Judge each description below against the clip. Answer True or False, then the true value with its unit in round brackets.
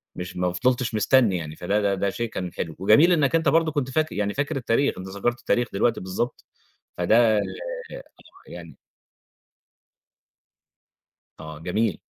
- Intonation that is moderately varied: False (5.8 semitones)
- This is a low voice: True (110 Hz)